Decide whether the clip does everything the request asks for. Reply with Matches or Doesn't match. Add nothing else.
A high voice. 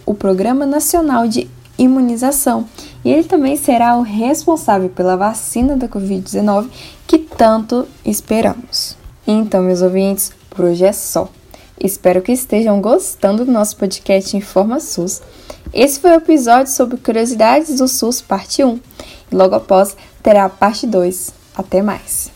Matches